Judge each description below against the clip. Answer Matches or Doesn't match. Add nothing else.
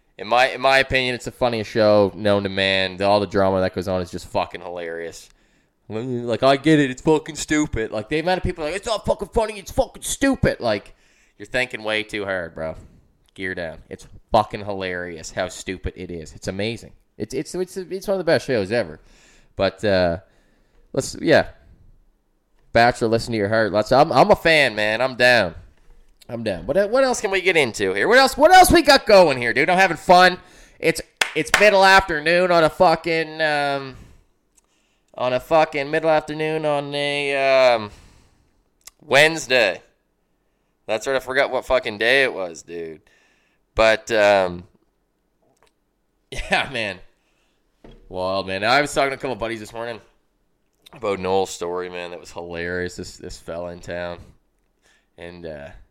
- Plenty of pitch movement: Matches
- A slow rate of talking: Doesn't match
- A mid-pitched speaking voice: Doesn't match